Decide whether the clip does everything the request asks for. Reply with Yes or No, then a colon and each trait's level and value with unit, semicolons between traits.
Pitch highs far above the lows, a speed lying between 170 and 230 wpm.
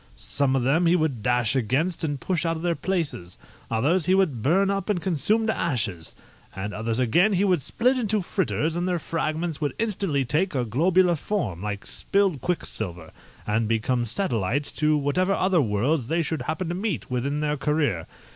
Yes: wide, 6.9 semitones; average, 190 wpm